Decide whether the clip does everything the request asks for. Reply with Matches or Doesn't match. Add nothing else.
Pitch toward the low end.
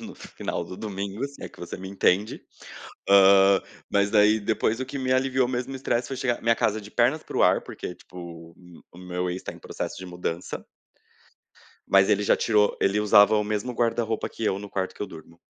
Matches